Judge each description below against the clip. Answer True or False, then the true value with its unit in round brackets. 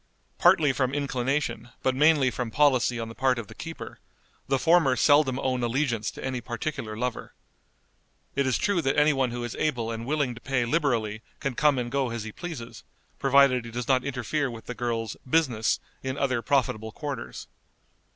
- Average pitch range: True (3.1 semitones)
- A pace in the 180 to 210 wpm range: True (185 wpm)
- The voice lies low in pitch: True (130 Hz)